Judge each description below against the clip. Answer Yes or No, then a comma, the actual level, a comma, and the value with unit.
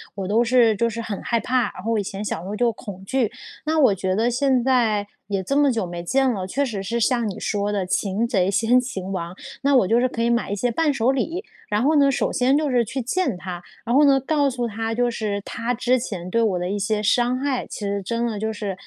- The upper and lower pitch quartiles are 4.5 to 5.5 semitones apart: No, average, 4.0 semitones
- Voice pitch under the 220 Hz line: No, high, 230 Hz